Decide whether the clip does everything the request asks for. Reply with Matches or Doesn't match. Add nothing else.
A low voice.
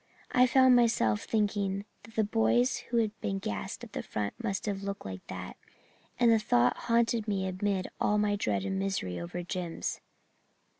Doesn't match